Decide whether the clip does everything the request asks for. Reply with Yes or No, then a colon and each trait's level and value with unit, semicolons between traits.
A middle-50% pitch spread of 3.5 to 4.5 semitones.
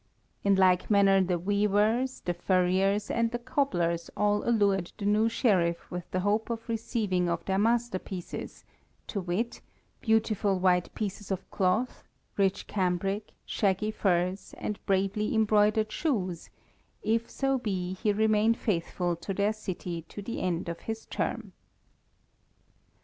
No: average, 3.1 semitones